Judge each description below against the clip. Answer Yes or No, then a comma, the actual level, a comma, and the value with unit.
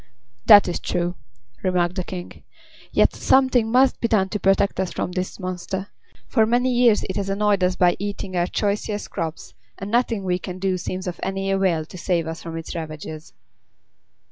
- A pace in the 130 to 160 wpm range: No, average, 185 wpm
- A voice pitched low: No, high, 190 Hz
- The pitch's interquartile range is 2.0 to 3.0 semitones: Yes, average, 2.7 semitones